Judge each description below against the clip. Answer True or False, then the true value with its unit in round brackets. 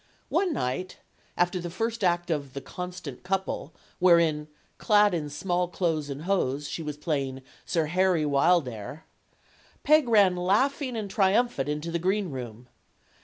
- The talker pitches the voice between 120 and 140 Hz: False (175 Hz)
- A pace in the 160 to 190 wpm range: False (140 wpm)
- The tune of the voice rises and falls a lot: False (4.7 semitones)